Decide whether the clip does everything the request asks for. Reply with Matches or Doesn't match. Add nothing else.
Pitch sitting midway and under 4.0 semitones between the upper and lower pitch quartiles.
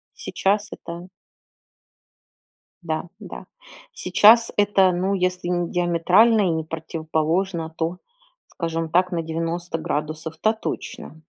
Matches